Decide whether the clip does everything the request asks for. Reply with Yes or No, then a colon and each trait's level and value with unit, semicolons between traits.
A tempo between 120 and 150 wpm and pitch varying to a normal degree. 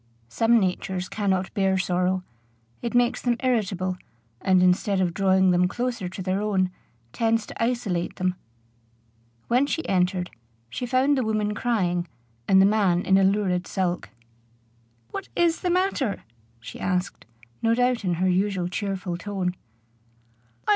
Yes: average, 145 wpm; average, 4.0 semitones